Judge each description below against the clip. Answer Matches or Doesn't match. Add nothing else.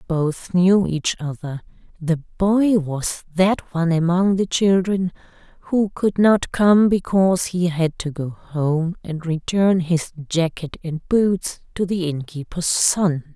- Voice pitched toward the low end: Doesn't match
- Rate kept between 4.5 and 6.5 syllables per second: Doesn't match